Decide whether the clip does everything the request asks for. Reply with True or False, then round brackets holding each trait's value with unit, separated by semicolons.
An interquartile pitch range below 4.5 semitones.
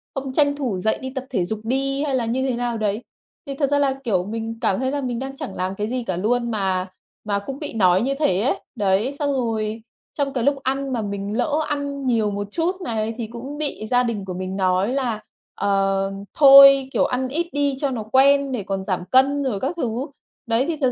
False (4.8 semitones)